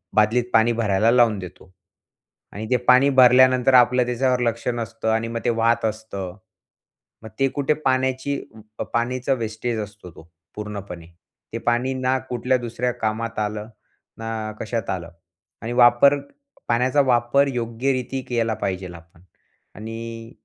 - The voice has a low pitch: Yes, low, 115 Hz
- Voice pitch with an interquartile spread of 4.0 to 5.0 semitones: No, narrow, 2.5 semitones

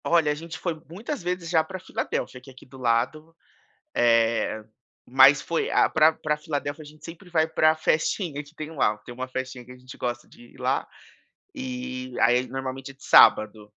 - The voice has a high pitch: No, medium, 150 Hz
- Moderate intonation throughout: Yes, average, 4.5 semitones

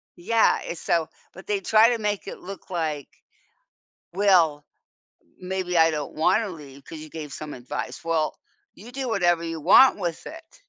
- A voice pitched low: No, medium, 175 Hz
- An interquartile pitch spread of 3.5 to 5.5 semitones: Yes, average, 4.6 semitones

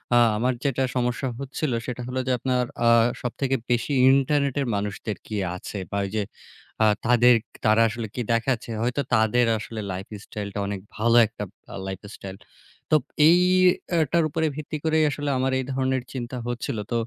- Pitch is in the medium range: No, low, 125 Hz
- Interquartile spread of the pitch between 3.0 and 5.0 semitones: Yes, average, 3.8 semitones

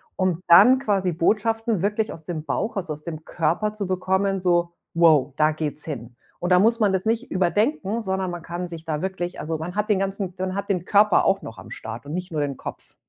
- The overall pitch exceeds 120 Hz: Yes, medium, 185 Hz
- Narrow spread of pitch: No, average, 3.7 semitones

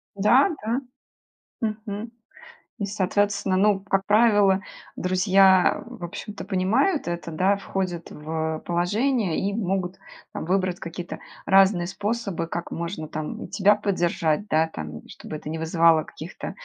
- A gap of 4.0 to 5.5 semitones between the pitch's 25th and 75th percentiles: No, average, 3.2 semitones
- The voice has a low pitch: No, high, 190 Hz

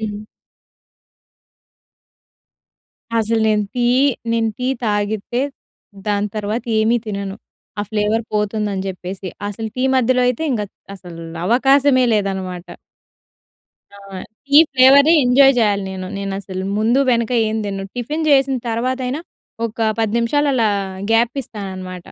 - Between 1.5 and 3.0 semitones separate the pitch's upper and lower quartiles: No, average, 3.7 semitones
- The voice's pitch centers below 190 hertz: No, high, 220 Hz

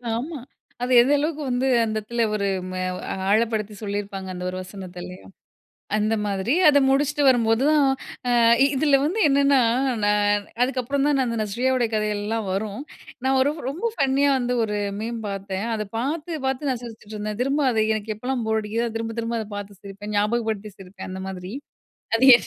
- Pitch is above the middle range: Yes, high, 225 Hz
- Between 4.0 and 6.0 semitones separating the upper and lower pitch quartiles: Yes, average, 4.4 semitones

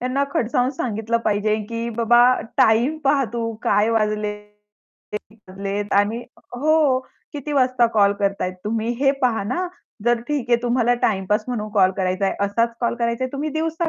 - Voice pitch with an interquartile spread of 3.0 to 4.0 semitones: Yes, average, 3.4 semitones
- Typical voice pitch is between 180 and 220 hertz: No, high, 235 Hz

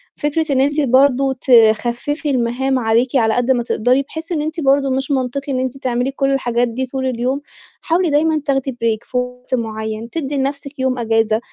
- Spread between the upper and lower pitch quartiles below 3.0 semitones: Yes, narrow, 2.6 semitones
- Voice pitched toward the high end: Yes, very high, 260 Hz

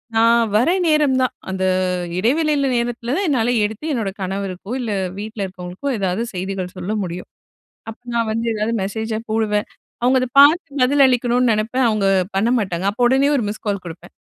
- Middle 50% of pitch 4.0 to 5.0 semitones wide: Yes, average, 4.3 semitones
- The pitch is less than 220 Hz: No, high, 225 Hz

